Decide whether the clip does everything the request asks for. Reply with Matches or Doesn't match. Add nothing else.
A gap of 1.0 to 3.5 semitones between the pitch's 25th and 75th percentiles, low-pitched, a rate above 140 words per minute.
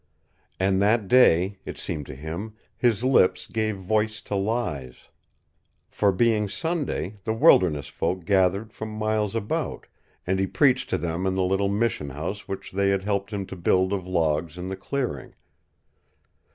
Matches